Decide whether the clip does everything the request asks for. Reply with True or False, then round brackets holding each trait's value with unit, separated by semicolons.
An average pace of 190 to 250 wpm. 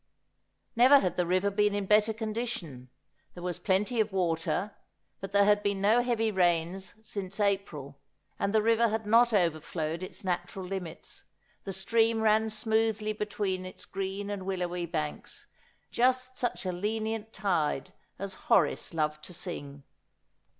False (150 wpm)